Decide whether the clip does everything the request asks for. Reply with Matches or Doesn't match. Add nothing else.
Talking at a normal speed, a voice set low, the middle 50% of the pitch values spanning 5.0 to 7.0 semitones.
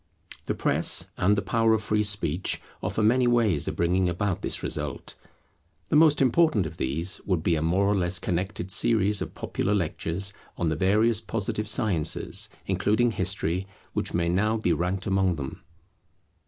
Doesn't match